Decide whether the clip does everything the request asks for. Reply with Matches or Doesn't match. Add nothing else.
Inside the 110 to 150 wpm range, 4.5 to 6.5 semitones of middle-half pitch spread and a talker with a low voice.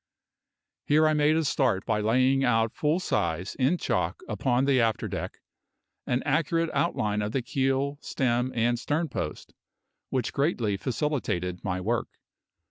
Matches